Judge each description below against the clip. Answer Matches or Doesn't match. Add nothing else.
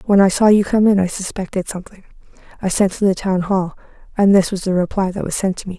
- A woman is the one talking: Matches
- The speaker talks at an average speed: Doesn't match